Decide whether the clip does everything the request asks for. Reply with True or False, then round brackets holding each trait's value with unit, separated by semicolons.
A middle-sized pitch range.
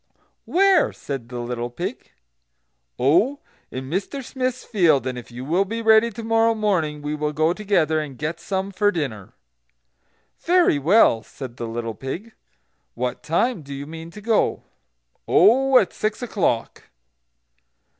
False (8.5 semitones)